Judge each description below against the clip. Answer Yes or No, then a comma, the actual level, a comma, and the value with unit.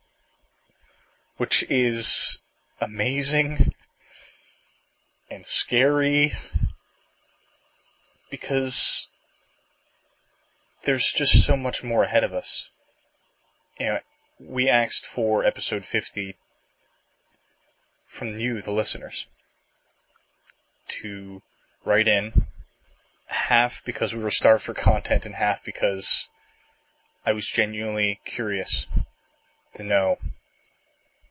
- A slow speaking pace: Yes, slow, 85 wpm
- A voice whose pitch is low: Yes, low, 115 Hz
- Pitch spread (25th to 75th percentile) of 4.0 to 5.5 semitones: Yes, average, 4.6 semitones